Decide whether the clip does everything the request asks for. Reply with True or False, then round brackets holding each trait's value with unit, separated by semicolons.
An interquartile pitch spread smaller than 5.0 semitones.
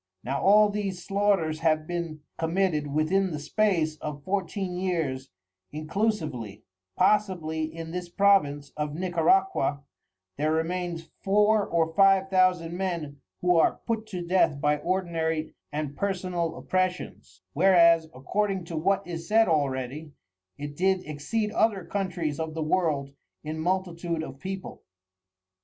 True (3.6 semitones)